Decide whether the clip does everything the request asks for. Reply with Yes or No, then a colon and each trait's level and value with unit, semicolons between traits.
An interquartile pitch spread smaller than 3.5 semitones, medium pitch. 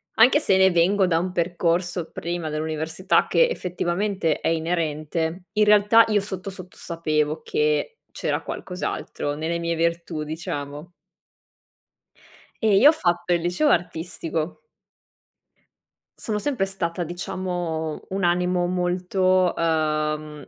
Yes: narrow, 2.6 semitones; medium, 175 Hz